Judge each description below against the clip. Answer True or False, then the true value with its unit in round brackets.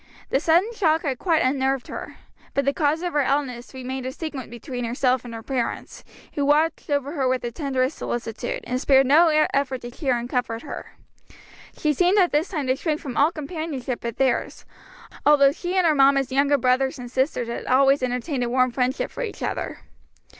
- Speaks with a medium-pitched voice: False (270 Hz)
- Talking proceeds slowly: False (200 wpm)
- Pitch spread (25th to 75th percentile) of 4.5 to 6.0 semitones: False (3.0 semitones)